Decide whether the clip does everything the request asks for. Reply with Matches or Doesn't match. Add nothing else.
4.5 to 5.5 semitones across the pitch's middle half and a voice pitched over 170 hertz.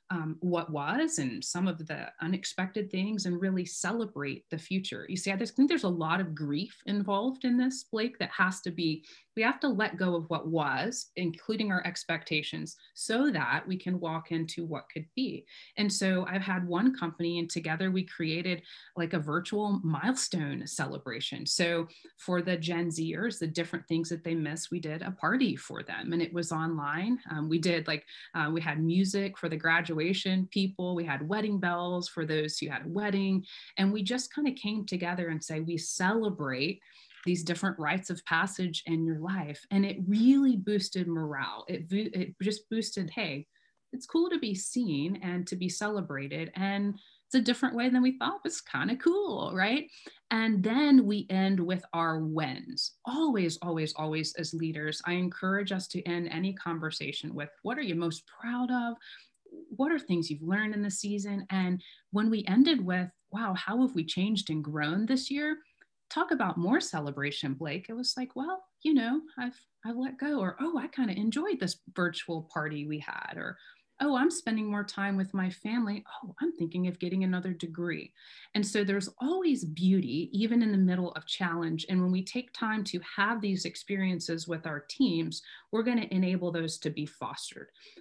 Matches